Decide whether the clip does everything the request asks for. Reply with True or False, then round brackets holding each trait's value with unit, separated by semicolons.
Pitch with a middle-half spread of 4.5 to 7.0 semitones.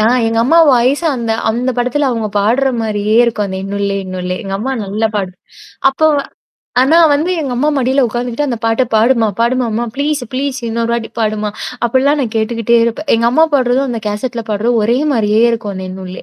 False (3.4 semitones)